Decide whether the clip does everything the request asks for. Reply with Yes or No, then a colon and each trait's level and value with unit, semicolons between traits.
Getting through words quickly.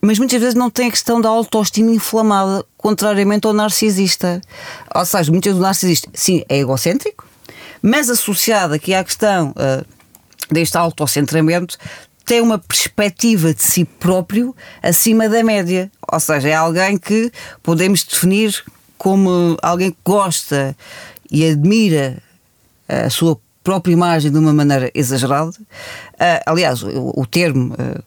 No: average, 140 wpm